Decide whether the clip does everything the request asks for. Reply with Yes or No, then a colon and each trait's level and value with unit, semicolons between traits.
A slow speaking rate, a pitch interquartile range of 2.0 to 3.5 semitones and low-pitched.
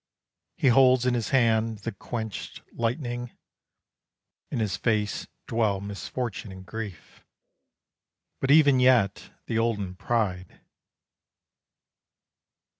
Yes: slow, 100 wpm; average, 3.2 semitones; low, 115 Hz